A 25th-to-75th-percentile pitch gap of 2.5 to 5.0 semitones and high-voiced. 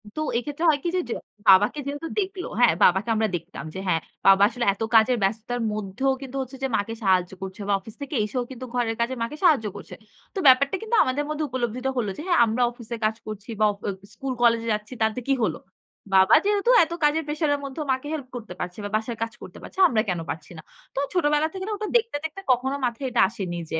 No: wide, 5.4 semitones; high, 245 Hz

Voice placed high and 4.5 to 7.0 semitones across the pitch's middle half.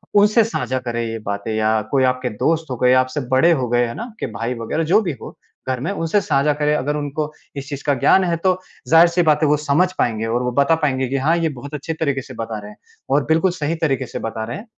No: medium, 140 Hz; average, 5.0 semitones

